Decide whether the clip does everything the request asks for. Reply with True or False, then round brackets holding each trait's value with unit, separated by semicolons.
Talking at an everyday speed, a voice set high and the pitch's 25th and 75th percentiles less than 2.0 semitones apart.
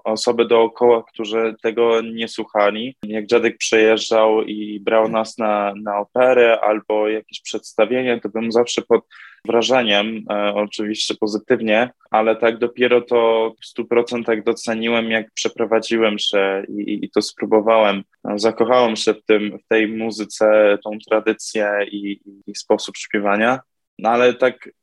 False (140 wpm; 110 Hz; 1.5 semitones)